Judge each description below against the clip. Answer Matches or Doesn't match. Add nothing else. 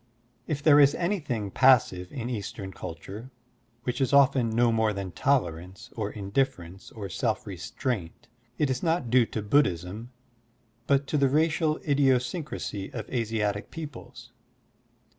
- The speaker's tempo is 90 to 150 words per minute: Matches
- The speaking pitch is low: Matches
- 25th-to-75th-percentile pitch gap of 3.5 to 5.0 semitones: Doesn't match